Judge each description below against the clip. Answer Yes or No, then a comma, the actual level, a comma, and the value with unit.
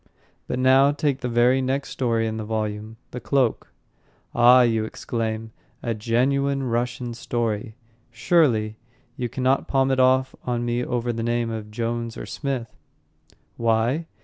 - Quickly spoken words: No, average, 150 wpm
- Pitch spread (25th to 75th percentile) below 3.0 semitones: Yes, narrow, 2.4 semitones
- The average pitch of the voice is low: Yes, low, 120 Hz